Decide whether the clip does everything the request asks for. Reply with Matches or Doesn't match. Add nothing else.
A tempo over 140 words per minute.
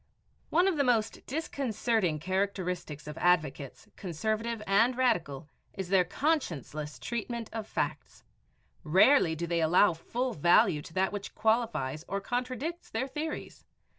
Doesn't match